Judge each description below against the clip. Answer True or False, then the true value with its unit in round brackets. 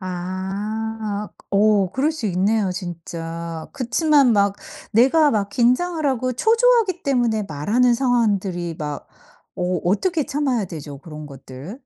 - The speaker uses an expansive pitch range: True (6.6 semitones)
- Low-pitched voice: False (210 Hz)